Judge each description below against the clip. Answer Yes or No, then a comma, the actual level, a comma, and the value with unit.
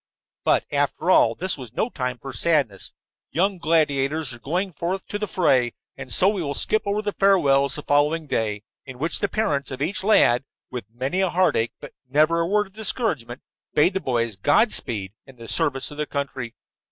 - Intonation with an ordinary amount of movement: No, wide, 6.6 semitones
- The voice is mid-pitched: Yes, medium, 145 Hz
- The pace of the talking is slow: No, average, 195 wpm